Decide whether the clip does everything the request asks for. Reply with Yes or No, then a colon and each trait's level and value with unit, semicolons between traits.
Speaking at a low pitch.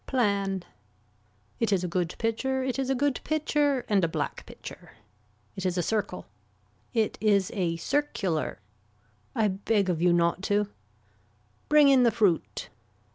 No: high, 210 Hz